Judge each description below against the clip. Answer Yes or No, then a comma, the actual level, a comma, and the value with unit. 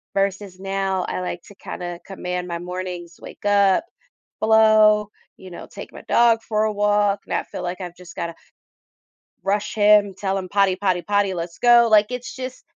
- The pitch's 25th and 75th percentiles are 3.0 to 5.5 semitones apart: No, narrow, 2.6 semitones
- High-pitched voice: Yes, high, 195 Hz